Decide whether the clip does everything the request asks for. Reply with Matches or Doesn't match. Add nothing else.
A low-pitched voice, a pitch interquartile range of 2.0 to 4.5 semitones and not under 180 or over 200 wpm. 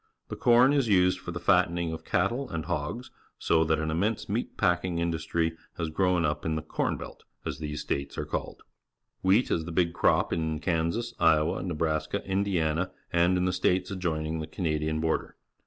Matches